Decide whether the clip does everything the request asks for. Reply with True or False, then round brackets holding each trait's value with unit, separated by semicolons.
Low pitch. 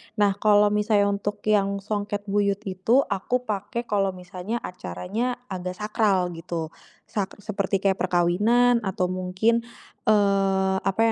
False (200 Hz)